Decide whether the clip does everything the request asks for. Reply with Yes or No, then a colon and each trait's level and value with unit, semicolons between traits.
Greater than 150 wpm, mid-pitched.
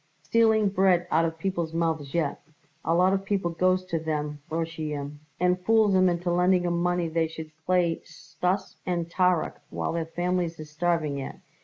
Yes: average, 175 wpm; medium, 170 Hz